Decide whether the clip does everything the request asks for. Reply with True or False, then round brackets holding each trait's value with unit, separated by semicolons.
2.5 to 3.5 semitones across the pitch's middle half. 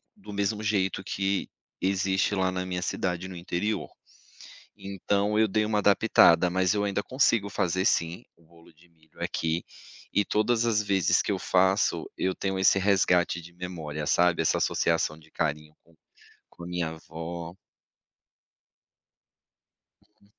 True (2.9 semitones)